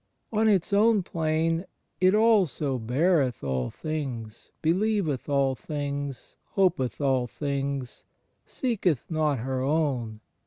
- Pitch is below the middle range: No, medium, 145 Hz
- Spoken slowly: Yes, slow, 110 wpm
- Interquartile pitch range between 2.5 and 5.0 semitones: No, wide, 5.4 semitones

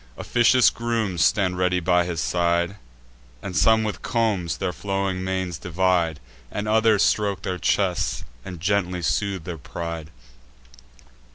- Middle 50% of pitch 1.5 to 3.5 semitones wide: Yes, average, 2.7 semitones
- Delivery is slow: Yes, slow, 130 wpm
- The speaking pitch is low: Yes, very low, 95 Hz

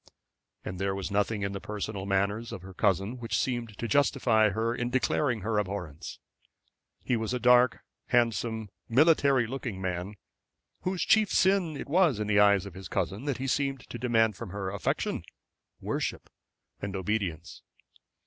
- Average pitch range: Yes, average, 4.1 semitones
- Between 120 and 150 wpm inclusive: No, average, 165 wpm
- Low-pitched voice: Yes, low, 110 Hz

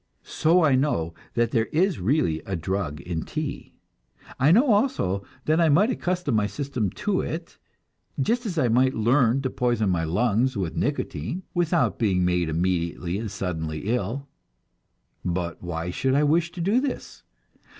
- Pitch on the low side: Yes, low, 120 Hz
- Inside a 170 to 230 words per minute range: No, average, 160 wpm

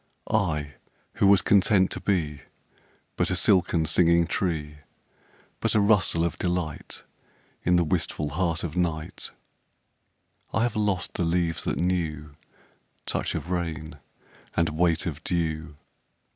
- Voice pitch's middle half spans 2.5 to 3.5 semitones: Yes, average, 2.8 semitones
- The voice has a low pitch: Yes, very low, 85 Hz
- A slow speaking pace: Yes, slow, 130 wpm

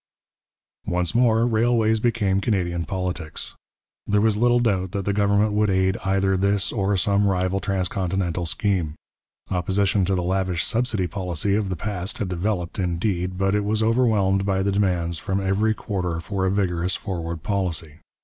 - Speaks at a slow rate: No, average, 160 wpm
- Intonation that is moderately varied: No, narrow, 2.3 semitones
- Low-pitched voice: Yes, very low, 95 Hz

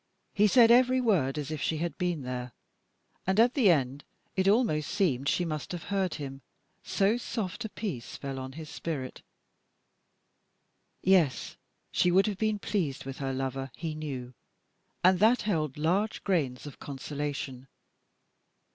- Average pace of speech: Yes, average, 155 wpm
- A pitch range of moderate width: No, wide, 6.5 semitones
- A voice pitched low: No, medium, 160 Hz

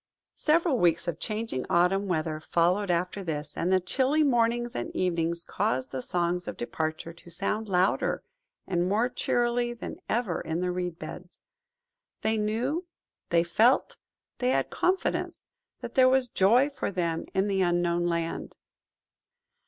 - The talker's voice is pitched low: No, medium, 185 Hz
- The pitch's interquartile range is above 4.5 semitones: Yes, wide, 5.6 semitones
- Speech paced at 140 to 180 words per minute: Yes, average, 150 wpm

